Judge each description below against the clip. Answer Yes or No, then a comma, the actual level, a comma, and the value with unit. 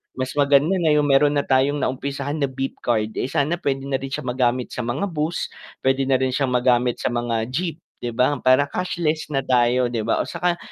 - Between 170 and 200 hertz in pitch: No, low, 135 Hz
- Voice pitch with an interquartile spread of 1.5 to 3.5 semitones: Yes, narrow, 2.6 semitones